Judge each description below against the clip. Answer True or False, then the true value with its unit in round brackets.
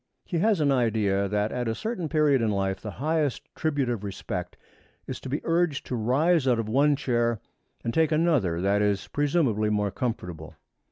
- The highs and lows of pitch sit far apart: True (6.5 semitones)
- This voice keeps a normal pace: True (185 wpm)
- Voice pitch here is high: False (120 Hz)